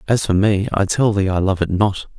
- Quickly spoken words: Yes, fast, 275 wpm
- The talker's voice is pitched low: Yes, low, 100 Hz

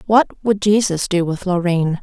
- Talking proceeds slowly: No, average, 180 wpm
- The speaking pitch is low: No, high, 190 Hz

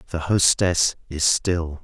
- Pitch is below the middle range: Yes, very low, 85 Hz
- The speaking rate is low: Yes, slow, 130 wpm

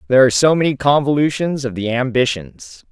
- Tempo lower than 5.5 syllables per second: No, 5.6 syllables/s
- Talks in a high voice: No, low, 125 Hz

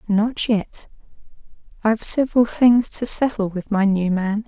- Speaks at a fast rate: No, average, 150 wpm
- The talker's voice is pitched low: No, high, 215 Hz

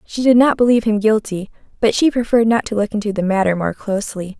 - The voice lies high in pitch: Yes, high, 215 Hz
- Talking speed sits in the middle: No, fast, 230 wpm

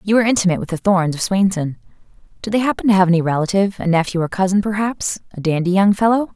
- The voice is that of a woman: Yes, female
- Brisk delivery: Yes, fast, 225 wpm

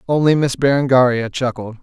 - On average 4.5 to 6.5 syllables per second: Yes, 5.4 syllables/s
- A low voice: Yes, low, 130 Hz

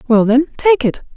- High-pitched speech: Yes, very high, 270 Hz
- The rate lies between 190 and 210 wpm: Yes, fast, 205 wpm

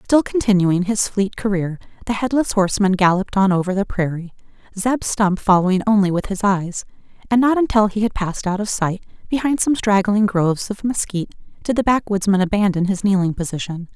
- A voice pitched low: No, high, 200 Hz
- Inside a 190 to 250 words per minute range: No, average, 175 wpm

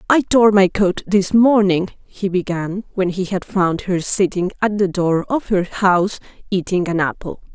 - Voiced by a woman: Yes, female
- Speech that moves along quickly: No, average, 185 wpm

